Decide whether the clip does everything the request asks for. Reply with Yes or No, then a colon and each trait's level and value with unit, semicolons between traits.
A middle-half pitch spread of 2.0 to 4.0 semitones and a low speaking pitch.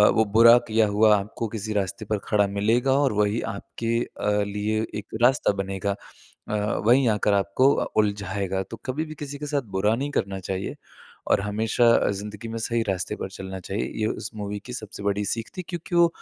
Yes: narrow, 2.5 semitones; low, 105 Hz